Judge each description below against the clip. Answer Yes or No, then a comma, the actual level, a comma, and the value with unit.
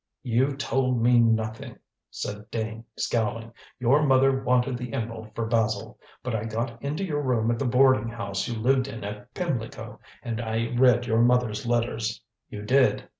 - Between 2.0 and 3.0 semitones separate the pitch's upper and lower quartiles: Yes, narrow, 2.4 semitones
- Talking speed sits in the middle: Yes, average, 170 wpm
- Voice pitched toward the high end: No, low, 120 Hz